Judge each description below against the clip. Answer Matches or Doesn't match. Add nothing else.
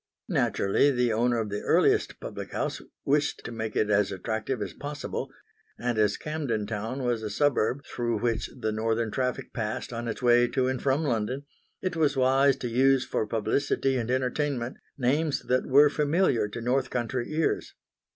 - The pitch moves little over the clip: Doesn't match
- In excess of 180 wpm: Doesn't match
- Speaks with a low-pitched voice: Matches